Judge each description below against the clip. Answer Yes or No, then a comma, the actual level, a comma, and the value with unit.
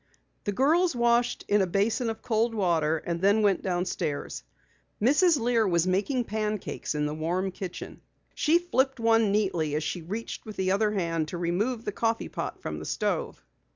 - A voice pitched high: Yes, high, 205 Hz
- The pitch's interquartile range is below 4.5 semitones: No, average, 4.8 semitones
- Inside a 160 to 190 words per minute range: Yes, average, 180 wpm